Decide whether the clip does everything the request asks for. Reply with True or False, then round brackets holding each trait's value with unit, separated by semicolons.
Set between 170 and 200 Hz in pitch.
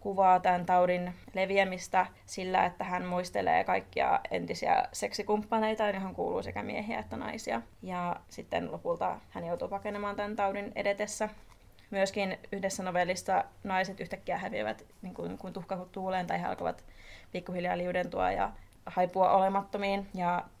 True (190 Hz)